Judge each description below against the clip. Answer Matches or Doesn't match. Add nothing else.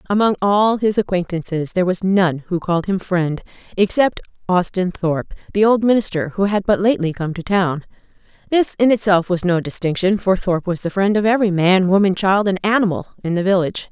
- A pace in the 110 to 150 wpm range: Doesn't match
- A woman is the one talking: Matches